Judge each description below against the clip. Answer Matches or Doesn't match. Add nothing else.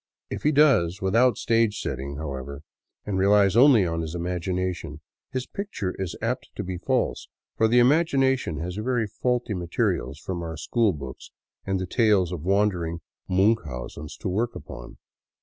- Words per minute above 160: Doesn't match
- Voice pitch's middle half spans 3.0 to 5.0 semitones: Doesn't match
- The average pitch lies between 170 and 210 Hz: Doesn't match